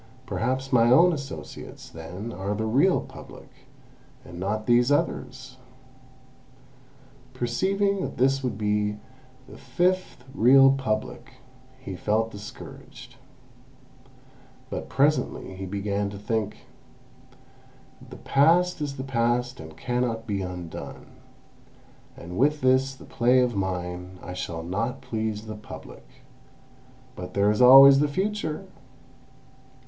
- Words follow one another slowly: Yes, slow, 115 wpm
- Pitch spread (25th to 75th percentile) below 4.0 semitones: No, average, 5.0 semitones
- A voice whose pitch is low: Yes, low, 120 Hz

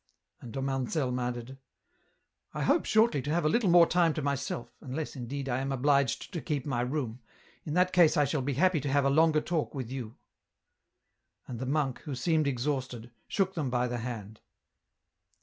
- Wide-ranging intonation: No, average, 3.7 semitones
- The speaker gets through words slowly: No, average, 195 wpm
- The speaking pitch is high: No, medium, 140 Hz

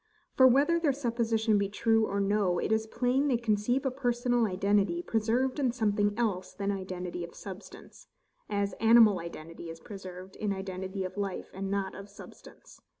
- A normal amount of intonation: Yes, average, 3.6 semitones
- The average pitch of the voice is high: Yes, high, 205 Hz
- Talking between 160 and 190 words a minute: Yes, average, 165 wpm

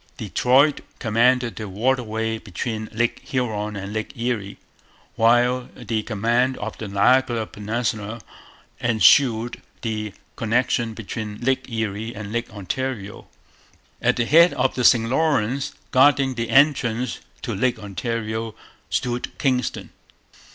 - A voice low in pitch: Yes, low, 115 Hz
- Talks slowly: Yes, slow, 120 wpm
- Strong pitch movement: No, average, 2.7 semitones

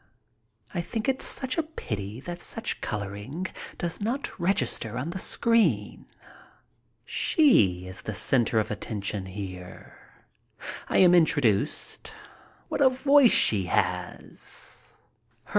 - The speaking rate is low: Yes, slow, 115 wpm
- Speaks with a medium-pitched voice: Yes, medium, 145 Hz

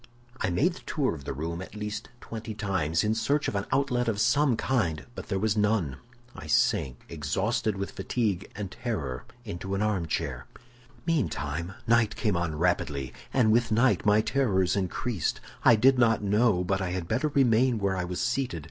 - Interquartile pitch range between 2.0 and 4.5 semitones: No, average, 5.1 semitones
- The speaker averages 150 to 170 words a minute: No, average, 185 wpm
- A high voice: No, low, 105 Hz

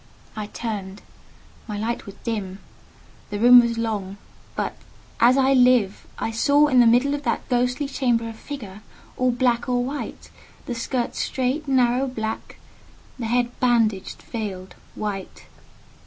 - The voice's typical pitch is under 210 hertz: No, high, 235 Hz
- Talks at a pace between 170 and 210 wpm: No, average, 140 wpm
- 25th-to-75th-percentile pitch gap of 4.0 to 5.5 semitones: No, average, 2.9 semitones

